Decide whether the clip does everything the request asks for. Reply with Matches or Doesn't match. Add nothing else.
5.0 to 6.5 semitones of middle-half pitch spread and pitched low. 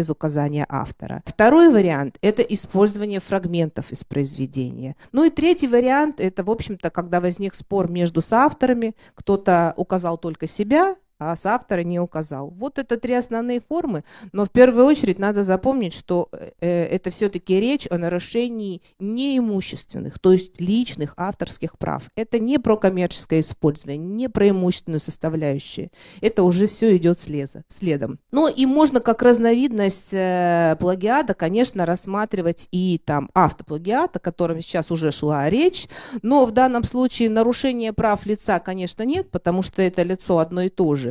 Doesn't match